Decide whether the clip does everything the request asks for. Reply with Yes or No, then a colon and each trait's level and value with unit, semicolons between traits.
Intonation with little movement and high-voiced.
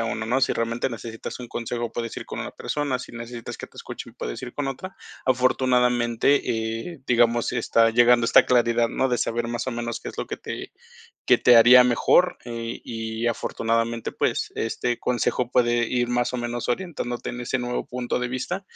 No: narrow, 1.2 semitones; low, 120 Hz